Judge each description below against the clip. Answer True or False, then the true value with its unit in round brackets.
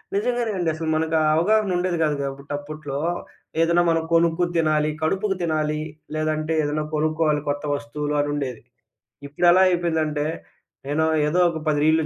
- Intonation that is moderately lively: False (2.3 semitones)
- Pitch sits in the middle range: True (155 Hz)